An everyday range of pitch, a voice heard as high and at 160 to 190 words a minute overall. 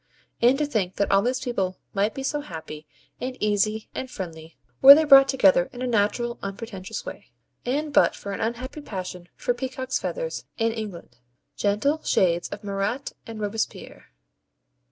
Yes: average, 4.8 semitones; high, 220 Hz; average, 165 wpm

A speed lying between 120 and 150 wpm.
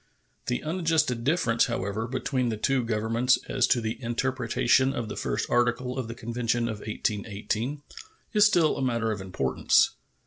No: average, 160 wpm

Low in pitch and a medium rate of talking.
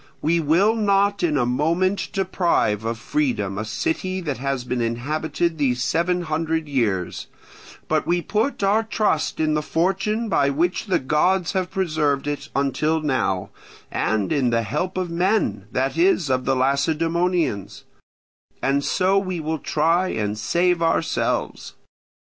No: medium, 160 Hz; average, 150 wpm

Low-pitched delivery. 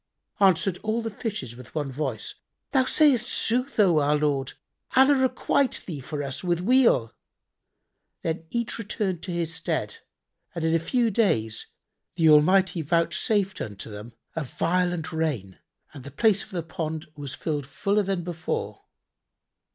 No: medium, 170 Hz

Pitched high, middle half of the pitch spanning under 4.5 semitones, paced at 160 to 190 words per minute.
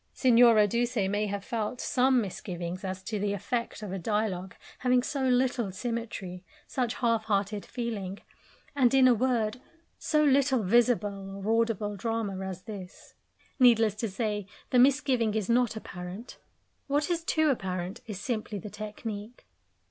No: high, 220 Hz; average, 3.7 semitones; average, 150 wpm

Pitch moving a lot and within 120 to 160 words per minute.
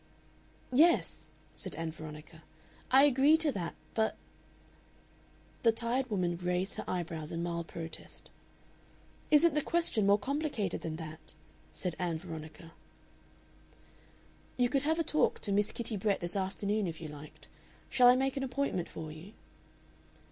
Yes: wide, 7.7 semitones; average, 150 wpm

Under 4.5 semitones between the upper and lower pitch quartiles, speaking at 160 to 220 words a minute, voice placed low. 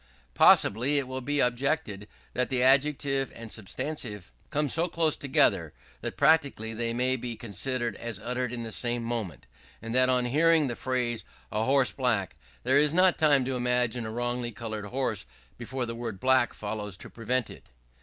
Yes: average, 2.8 semitones; average, 175 wpm; low, 125 Hz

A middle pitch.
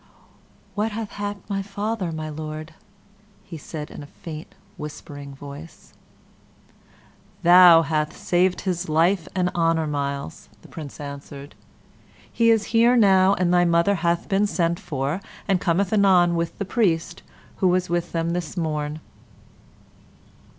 Yes: medium, 170 Hz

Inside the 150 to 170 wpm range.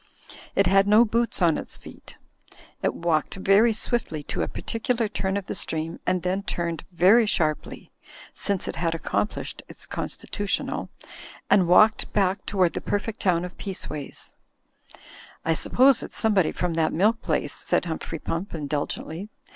Yes: average, 155 wpm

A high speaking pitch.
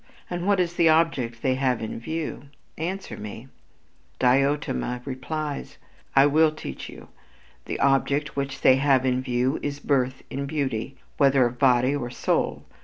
No: low, 135 Hz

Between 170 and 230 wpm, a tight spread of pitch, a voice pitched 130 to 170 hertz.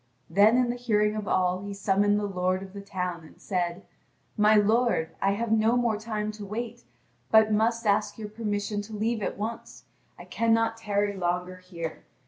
No: average, 185 wpm; narrow, 2.3 semitones; high, 210 Hz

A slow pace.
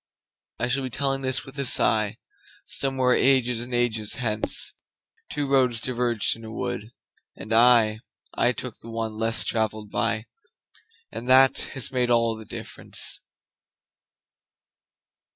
Yes: slow, 120 wpm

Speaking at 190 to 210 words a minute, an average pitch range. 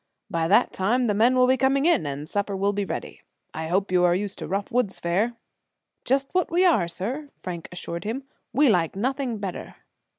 No: fast, 205 wpm; wide, 6.1 semitones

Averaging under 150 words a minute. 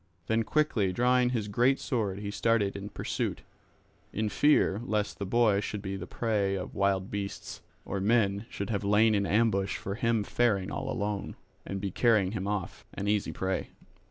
No: average, 180 wpm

